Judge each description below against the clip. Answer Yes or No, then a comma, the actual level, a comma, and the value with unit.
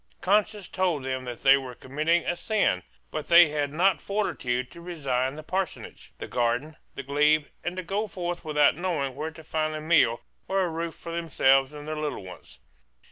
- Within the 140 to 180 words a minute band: No, average, 190 wpm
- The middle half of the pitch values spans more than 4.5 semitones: No, average, 4.2 semitones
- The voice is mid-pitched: Yes, medium, 155 Hz